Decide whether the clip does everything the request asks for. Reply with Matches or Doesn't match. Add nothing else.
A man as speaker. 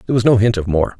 Matches